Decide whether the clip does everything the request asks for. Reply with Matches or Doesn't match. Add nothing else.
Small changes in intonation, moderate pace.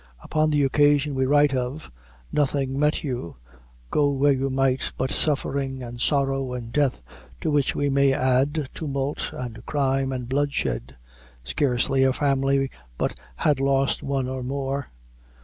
Matches